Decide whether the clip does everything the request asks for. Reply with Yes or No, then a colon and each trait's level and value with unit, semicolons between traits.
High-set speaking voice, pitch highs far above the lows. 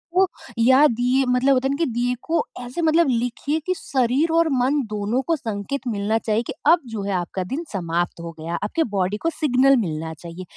Yes: high, 245 Hz; wide, 5.7 semitones